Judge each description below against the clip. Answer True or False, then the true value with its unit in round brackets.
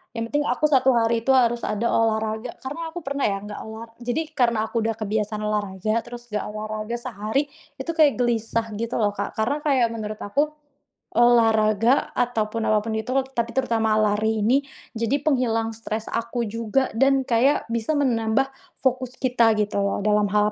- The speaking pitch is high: True (230 Hz)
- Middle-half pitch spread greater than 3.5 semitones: False (2.8 semitones)